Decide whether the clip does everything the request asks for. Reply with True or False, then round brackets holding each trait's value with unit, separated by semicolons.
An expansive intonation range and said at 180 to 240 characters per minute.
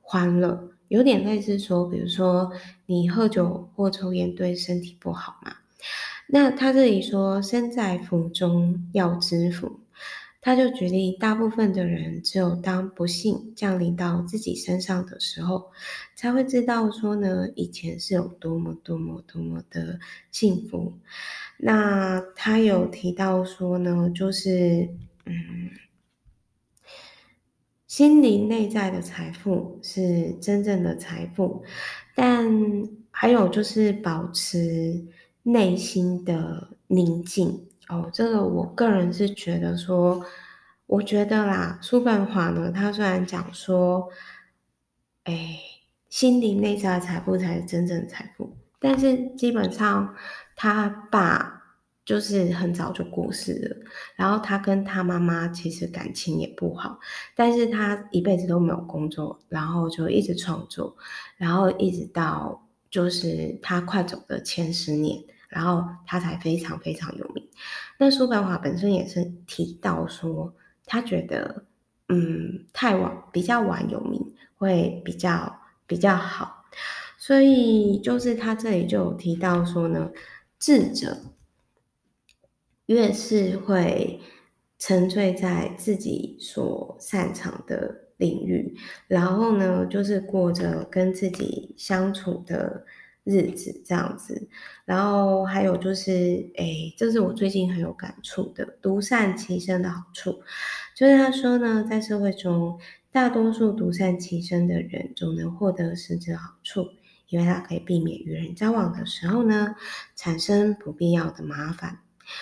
False (3.1 semitones; 195 characters per minute)